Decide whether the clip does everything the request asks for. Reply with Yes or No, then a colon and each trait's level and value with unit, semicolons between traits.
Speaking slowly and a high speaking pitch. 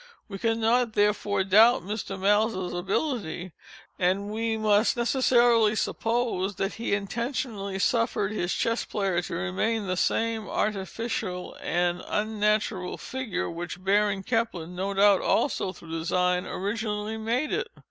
Yes: slow, 125 wpm; high, 205 Hz